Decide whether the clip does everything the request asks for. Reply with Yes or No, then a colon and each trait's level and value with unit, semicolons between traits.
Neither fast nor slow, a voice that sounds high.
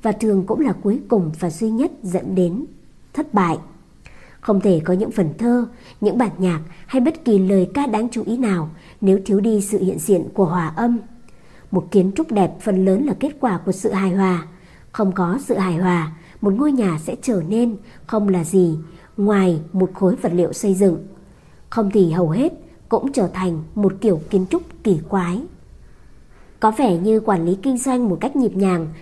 Yes: average, 205 wpm; high, 195 Hz